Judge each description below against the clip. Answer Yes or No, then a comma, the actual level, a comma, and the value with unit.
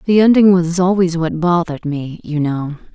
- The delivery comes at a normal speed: Yes, average, 185 wpm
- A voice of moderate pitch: Yes, medium, 170 Hz